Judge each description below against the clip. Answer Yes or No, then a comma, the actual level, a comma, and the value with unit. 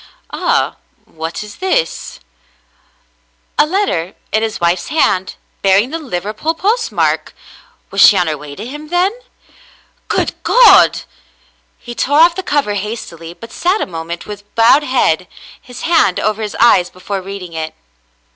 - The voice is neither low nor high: No, high, 215 Hz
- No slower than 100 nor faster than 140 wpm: No, average, 155 wpm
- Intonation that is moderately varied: No, wide, 9.0 semitones